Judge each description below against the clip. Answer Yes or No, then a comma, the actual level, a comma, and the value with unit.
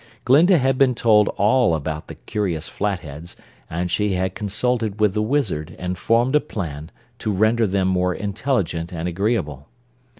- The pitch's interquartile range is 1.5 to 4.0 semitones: No, average, 5.0 semitones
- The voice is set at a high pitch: No, low, 100 Hz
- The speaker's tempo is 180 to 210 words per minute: No, average, 160 wpm